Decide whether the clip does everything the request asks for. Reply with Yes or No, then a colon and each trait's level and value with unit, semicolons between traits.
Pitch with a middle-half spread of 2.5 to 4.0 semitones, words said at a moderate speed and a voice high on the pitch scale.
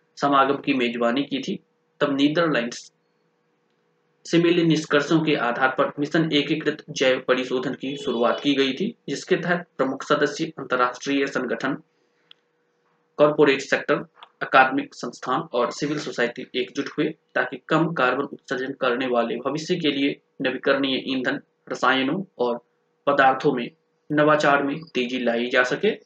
No: average, 2.8 semitones; average, 135 wpm; medium, 140 Hz